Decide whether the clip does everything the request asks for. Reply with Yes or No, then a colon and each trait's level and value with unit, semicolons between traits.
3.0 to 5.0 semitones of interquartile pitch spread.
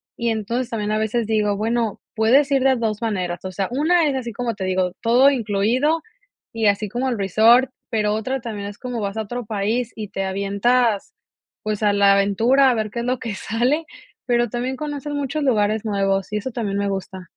Yes: average, 3.6 semitones